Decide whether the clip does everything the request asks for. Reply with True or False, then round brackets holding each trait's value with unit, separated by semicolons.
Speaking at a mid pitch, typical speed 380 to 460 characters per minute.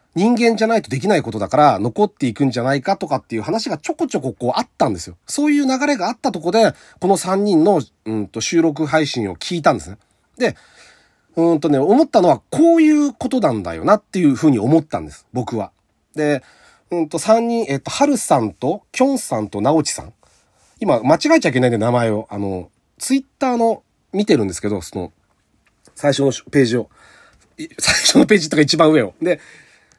True (160 Hz; 390 characters per minute)